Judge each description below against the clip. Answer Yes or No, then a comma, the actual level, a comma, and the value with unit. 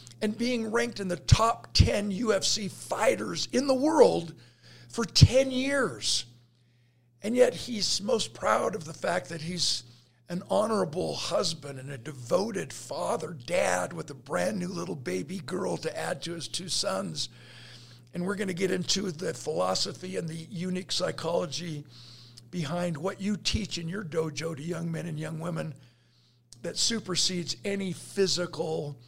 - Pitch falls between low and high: Yes, medium, 170 Hz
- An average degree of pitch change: No, wide, 6.4 semitones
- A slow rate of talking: No, average, 155 wpm